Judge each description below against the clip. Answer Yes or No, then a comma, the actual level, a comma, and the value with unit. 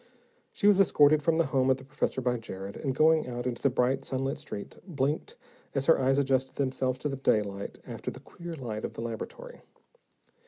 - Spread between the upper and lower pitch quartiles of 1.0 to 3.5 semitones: Yes, average, 3.1 semitones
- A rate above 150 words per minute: Yes, average, 200 wpm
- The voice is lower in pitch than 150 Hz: Yes, low, 135 Hz